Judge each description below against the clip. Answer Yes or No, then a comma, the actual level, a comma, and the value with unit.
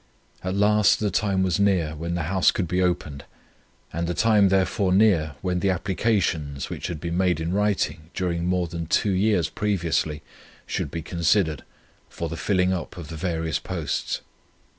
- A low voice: Yes, very low, 90 Hz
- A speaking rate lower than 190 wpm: Yes, average, 175 wpm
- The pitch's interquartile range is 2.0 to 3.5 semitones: Yes, average, 2.9 semitones